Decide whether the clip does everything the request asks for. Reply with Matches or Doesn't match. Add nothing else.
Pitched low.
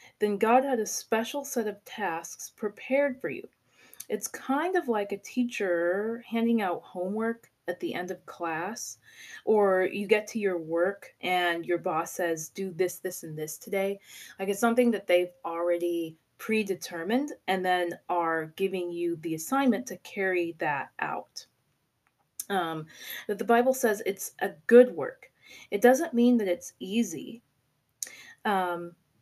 Doesn't match